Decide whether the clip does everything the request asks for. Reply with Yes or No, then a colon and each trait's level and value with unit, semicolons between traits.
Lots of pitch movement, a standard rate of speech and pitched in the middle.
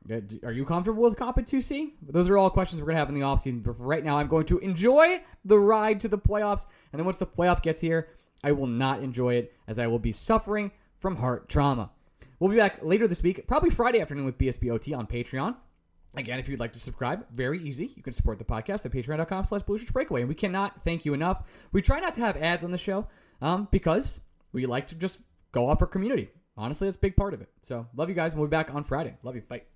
No: wide, 7.4 semitones; fast, 250 wpm; medium, 160 Hz